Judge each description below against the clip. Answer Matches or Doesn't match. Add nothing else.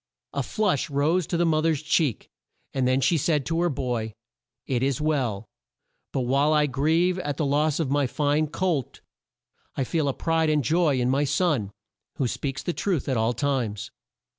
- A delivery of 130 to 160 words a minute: Doesn't match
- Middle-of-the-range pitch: Matches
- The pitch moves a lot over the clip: Doesn't match